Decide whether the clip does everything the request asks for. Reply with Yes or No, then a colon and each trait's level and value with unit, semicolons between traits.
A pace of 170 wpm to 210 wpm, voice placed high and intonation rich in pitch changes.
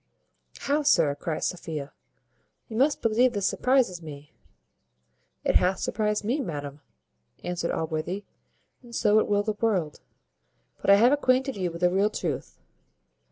No: average, 145 wpm; high, 200 Hz; wide, 5.8 semitones